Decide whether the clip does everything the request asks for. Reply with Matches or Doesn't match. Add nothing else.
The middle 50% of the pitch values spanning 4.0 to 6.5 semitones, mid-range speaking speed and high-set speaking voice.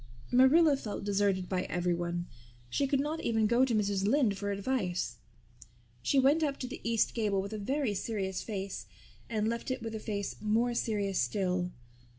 Matches